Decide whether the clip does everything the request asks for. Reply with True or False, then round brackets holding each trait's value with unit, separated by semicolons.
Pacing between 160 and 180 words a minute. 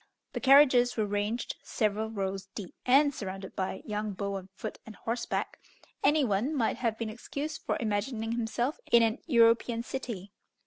True (165 wpm)